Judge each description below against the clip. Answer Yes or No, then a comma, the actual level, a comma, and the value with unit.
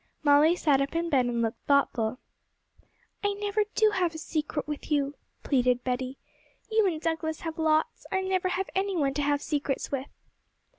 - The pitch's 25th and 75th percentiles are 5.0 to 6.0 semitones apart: No, average, 4.5 semitones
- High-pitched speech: Yes, very high, 305 Hz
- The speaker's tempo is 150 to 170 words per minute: No, average, 180 wpm